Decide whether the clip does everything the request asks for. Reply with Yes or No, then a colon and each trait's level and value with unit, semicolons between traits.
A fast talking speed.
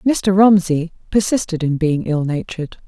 No: average, 145 wpm